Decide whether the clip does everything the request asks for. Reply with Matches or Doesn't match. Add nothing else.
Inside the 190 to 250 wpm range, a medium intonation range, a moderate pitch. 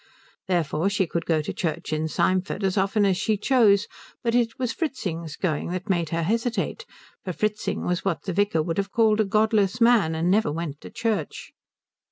Doesn't match